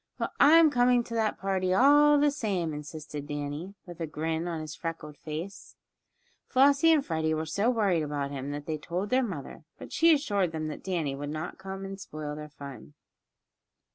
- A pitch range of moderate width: No, wide, 6.7 semitones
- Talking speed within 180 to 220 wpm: Yes, average, 190 wpm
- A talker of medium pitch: Yes, medium, 170 Hz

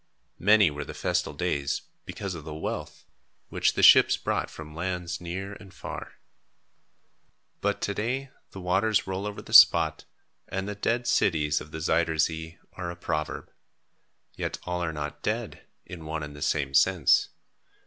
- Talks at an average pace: Yes, average, 165 wpm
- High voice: No, very low, 85 Hz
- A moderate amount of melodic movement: Yes, average, 4.0 semitones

